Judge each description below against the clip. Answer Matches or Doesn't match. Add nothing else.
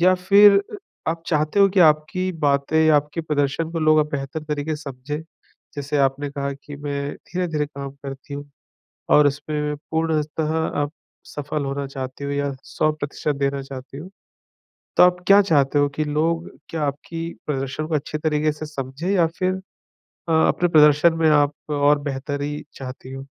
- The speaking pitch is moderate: Matches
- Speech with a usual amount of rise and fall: Doesn't match